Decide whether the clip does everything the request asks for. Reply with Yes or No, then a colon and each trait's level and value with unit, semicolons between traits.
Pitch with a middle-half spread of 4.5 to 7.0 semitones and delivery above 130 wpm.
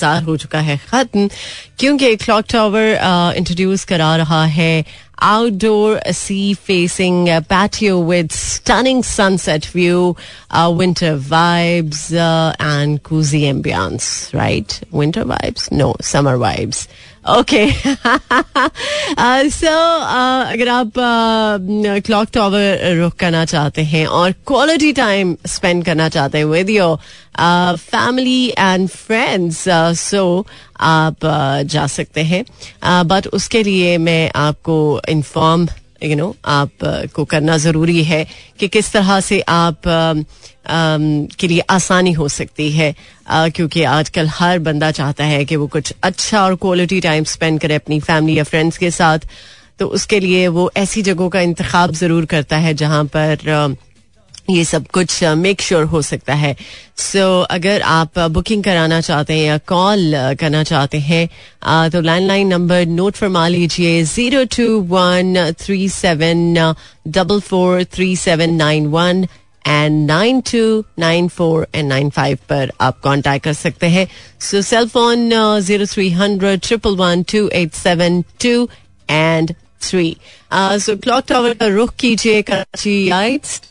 No: average, 4.0 semitones; average, 140 wpm